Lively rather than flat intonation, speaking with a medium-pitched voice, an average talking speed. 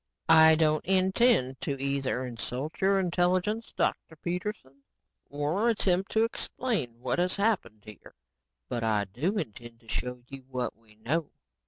Yes: wide, 7.3 semitones; medium, 150 Hz; average, 145 wpm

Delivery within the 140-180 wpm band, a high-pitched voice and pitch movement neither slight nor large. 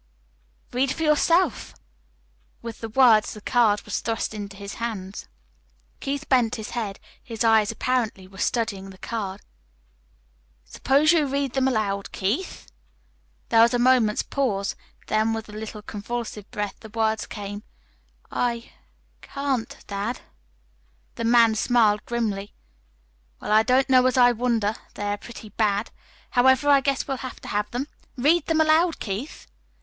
Yes: average, 150 wpm; high, 230 Hz; average, 3.7 semitones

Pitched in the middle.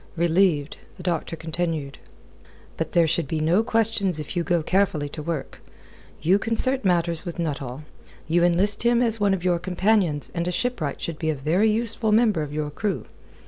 Yes: medium, 175 Hz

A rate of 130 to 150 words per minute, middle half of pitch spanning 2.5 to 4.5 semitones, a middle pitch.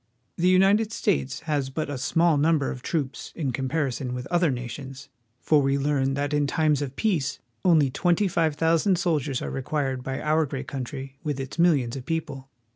No: average, 190 wpm; average, 3.4 semitones; medium, 145 Hz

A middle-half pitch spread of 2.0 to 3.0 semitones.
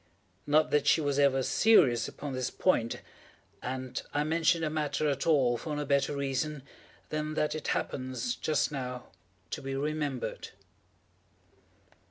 Yes: narrow, 2.6 semitones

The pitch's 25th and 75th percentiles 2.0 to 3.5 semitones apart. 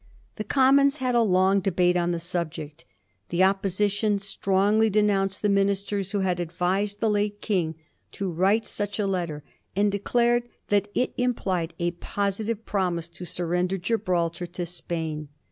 Yes: average, 2.9 semitones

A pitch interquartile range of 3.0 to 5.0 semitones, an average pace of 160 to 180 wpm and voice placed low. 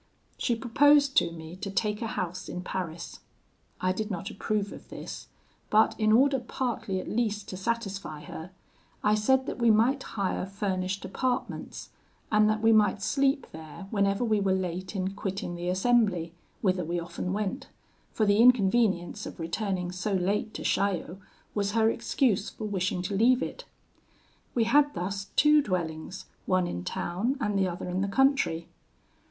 No: average, 3.7 semitones; average, 170 wpm; high, 200 Hz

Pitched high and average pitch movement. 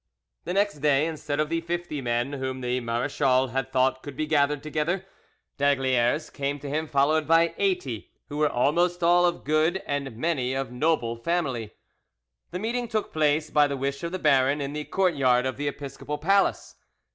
No: medium, 145 Hz; average, 3.8 semitones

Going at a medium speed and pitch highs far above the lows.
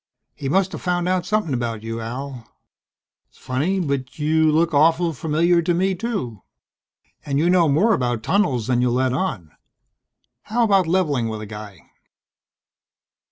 Yes: average, 150 wpm; wide, 6.4 semitones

